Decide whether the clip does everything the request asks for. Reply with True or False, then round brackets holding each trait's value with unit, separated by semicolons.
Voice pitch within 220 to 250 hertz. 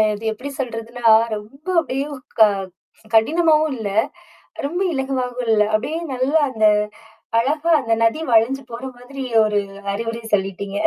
True (245 Hz)